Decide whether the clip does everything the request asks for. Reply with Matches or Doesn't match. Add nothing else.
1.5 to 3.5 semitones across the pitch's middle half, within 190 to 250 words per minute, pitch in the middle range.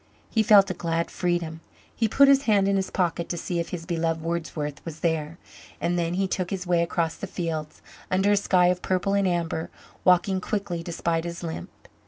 Matches